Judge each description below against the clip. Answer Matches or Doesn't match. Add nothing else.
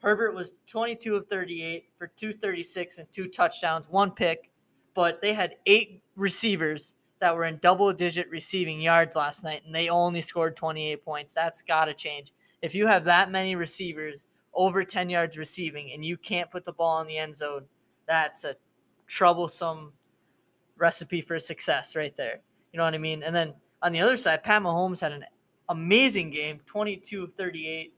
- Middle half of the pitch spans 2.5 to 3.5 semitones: Matches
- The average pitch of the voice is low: Doesn't match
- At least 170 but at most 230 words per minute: Matches